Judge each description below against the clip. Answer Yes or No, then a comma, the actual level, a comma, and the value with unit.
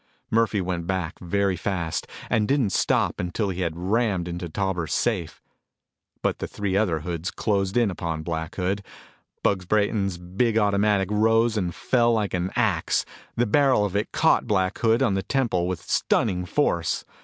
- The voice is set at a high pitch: No, very low, 95 Hz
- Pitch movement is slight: No, average, 3.6 semitones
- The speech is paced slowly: No, average, 170 wpm